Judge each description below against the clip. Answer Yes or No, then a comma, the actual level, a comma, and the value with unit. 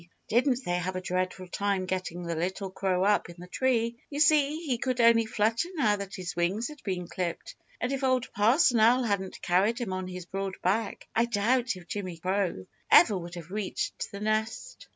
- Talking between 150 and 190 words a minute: No, average, 200 wpm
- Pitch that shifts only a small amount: No, average, 4.3 semitones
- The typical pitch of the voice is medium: No, high, 205 Hz